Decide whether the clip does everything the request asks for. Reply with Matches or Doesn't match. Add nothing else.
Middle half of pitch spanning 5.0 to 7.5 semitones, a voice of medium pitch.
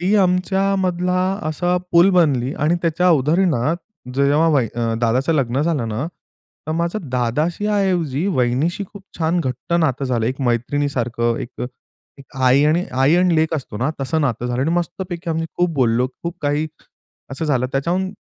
Matches